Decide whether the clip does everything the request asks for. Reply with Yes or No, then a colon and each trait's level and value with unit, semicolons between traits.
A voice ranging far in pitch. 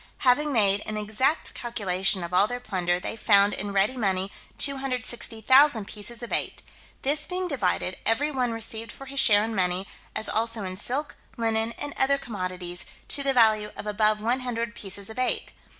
No: average, 4.2 semitones